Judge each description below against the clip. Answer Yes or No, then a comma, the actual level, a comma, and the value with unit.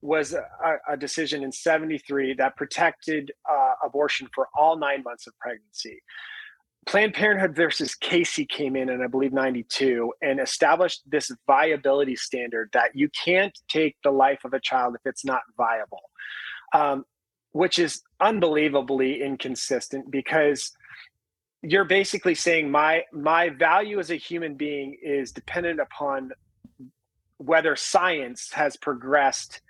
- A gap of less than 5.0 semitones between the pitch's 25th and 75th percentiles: Yes, average, 4.6 semitones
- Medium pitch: Yes, medium, 150 Hz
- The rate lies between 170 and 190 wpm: No, average, 140 wpm